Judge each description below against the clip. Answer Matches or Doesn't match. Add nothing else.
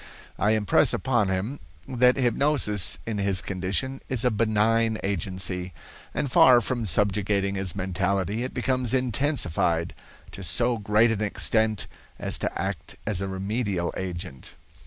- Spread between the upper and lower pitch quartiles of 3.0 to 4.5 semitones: Matches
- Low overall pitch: Matches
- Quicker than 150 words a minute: Doesn't match